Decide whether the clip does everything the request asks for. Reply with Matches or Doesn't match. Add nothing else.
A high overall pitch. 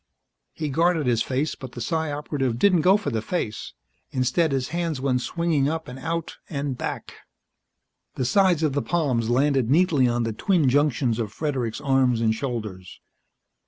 Doesn't match